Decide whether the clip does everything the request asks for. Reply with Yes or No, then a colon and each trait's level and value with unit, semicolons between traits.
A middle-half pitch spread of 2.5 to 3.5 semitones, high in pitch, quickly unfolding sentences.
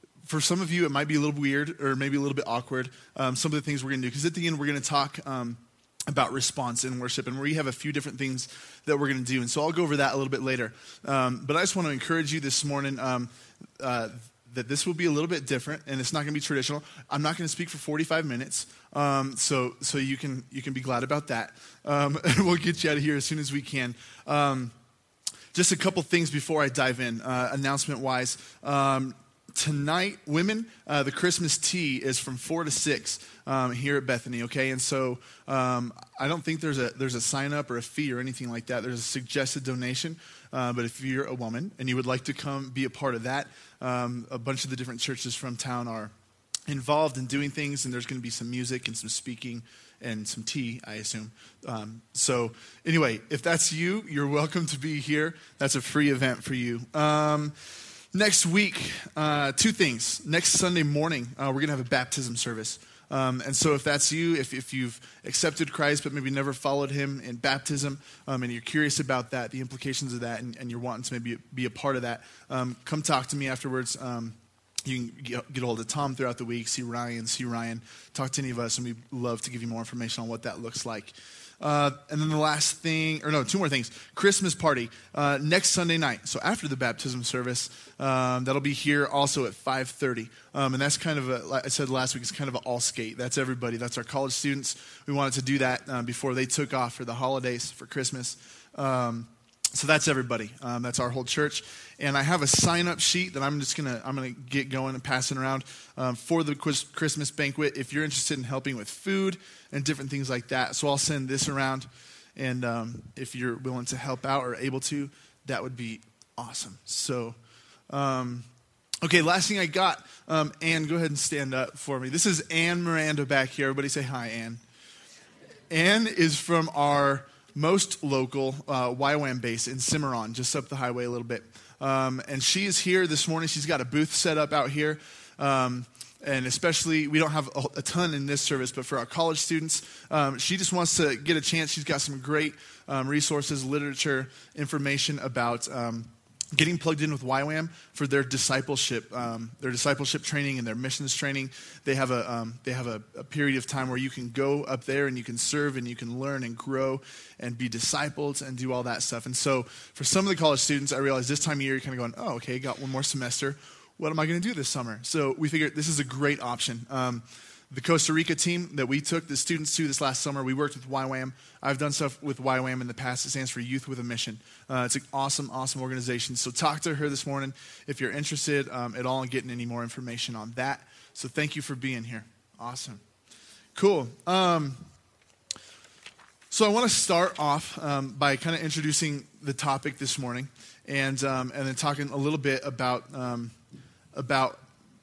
No: average, 3.0 semitones; low, 135 Hz; fast, 230 wpm